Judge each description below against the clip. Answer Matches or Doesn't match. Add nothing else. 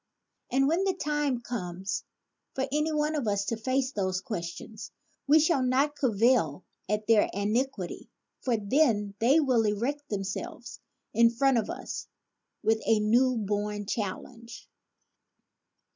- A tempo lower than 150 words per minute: Matches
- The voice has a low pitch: Doesn't match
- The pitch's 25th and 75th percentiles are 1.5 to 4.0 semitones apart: Doesn't match